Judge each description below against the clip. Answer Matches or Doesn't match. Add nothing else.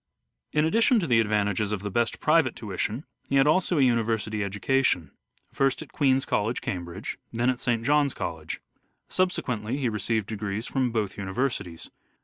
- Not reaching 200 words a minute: Matches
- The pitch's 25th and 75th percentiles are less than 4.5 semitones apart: Doesn't match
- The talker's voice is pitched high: Doesn't match